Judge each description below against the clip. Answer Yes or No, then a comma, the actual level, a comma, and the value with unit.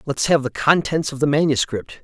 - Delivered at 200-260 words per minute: Yes, fast, 205 wpm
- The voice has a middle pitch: Yes, medium, 145 Hz